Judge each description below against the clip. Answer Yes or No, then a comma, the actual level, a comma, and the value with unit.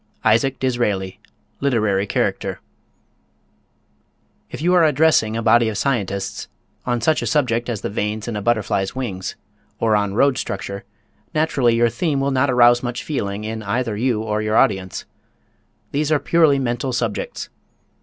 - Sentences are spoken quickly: No, average, 155 wpm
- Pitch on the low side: Yes, low, 120 Hz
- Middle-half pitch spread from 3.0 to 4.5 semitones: Yes, average, 4.2 semitones